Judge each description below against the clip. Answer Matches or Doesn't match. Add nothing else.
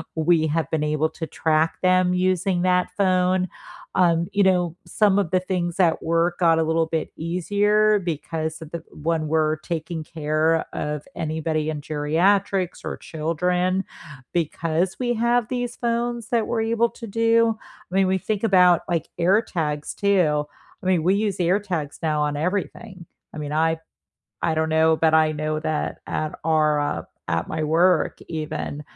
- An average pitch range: Matches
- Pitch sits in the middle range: Matches